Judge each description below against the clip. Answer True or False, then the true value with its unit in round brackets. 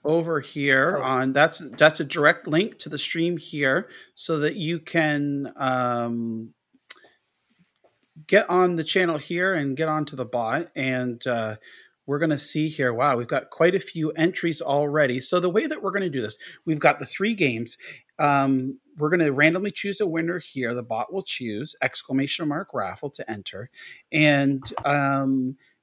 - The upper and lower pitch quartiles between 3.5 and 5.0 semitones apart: True (3.9 semitones)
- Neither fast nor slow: True (175 wpm)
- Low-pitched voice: False (150 Hz)